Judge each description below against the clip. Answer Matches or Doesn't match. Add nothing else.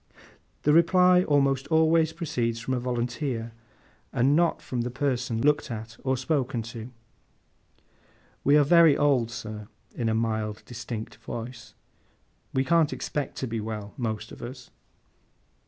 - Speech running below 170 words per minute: Matches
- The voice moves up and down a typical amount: Matches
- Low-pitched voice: Matches